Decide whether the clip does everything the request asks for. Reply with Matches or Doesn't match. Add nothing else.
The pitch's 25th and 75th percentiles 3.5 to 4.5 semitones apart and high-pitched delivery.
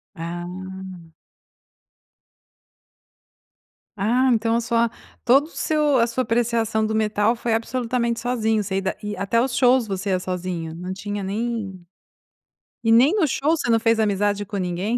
Matches